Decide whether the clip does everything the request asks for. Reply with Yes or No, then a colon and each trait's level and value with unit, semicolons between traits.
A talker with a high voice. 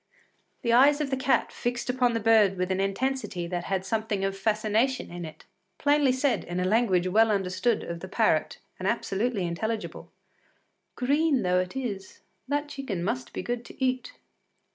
Yes: high, 220 Hz